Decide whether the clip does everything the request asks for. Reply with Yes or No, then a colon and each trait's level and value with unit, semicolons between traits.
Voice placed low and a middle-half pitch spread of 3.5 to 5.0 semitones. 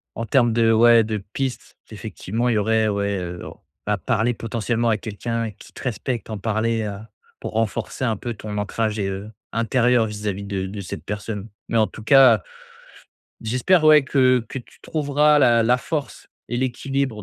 No: low, 115 Hz; average, 2.7 semitones